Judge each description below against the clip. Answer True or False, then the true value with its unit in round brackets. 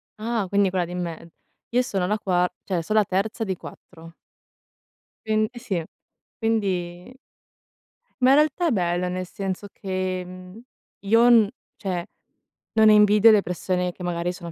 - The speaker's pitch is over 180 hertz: True (190 Hz)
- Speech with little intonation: False (3.3 semitones)